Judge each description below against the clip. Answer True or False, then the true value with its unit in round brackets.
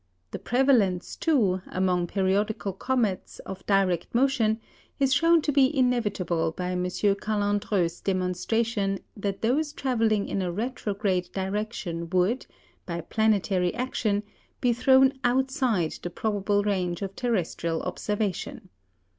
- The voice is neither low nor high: False (205 Hz)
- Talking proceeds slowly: True (120 wpm)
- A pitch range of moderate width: True (4.6 semitones)